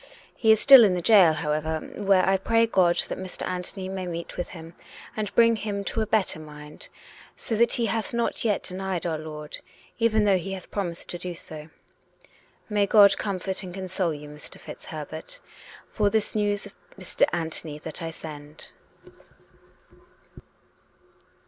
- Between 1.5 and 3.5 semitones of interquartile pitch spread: No, average, 4.2 semitones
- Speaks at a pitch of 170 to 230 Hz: Yes, high, 190 Hz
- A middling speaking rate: Yes, average, 170 wpm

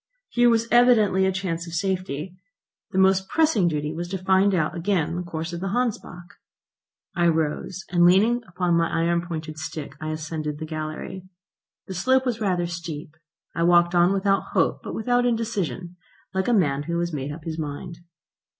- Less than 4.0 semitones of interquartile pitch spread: Yes, average, 3.1 semitones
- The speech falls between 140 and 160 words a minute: No, average, 180 wpm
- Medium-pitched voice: Yes, medium, 175 Hz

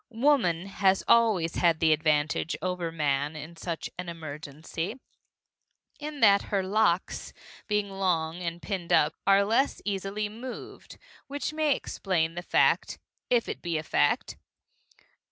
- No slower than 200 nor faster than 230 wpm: No, slow, 135 wpm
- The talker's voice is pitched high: No, medium, 180 Hz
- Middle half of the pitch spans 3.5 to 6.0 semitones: Yes, average, 4.4 semitones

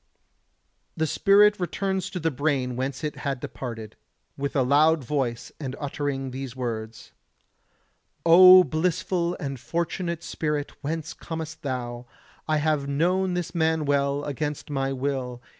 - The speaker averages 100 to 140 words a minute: Yes, slow, 135 wpm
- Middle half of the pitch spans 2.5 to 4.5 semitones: Yes, average, 3.6 semitones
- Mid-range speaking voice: Yes, medium, 145 Hz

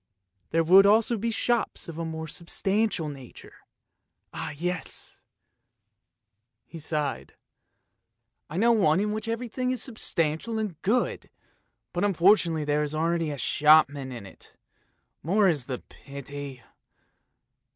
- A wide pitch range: Yes, wide, 6.3 semitones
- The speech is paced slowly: Yes, slow, 130 wpm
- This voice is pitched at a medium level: Yes, medium, 165 Hz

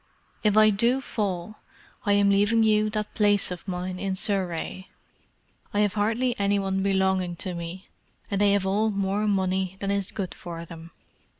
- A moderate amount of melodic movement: No, narrow, 2.0 semitones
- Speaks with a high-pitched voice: Yes, high, 200 Hz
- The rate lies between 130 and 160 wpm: No, average, 175 wpm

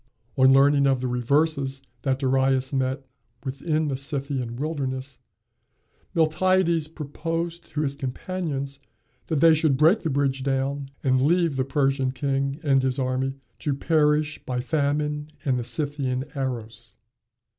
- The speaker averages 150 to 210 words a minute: No, slow, 135 wpm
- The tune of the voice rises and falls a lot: No, narrow, 2.5 semitones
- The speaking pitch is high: No, medium, 140 Hz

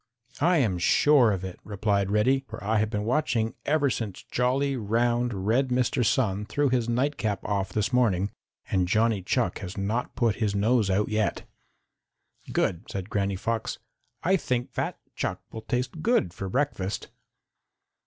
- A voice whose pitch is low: Yes, low, 110 Hz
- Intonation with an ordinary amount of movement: Yes, average, 4.0 semitones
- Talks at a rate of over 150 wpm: Yes, average, 160 wpm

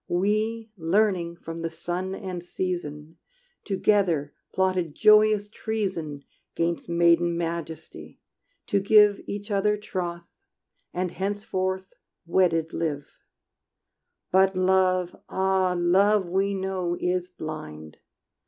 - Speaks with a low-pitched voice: No, medium, 185 Hz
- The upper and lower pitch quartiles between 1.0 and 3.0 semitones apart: Yes, narrow, 2.6 semitones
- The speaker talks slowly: Yes, slow, 100 wpm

